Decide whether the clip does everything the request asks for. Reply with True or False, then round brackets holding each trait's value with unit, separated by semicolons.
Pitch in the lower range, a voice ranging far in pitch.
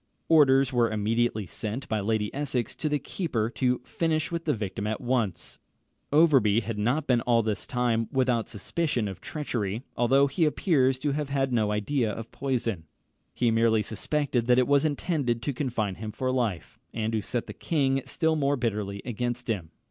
False (120 Hz; 4.2 semitones)